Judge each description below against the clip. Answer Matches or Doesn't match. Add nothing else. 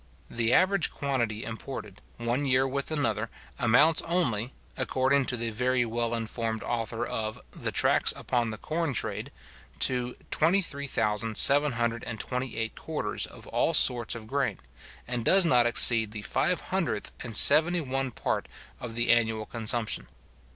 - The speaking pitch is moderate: Doesn't match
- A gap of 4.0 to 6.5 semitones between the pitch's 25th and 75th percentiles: Doesn't match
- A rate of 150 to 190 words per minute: Doesn't match